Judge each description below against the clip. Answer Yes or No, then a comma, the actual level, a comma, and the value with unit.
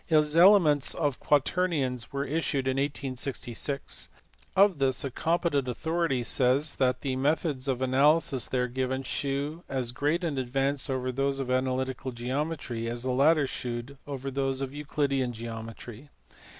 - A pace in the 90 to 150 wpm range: Yes, average, 145 wpm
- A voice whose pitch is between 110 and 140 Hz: Yes, low, 135 Hz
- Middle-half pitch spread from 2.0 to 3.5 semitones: Yes, narrow, 2.5 semitones